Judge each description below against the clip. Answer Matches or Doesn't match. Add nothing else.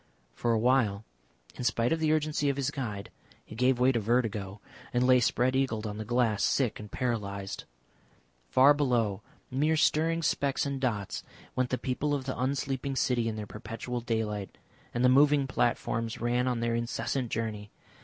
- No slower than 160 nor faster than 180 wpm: Matches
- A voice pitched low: Matches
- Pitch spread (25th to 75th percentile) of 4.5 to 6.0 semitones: Doesn't match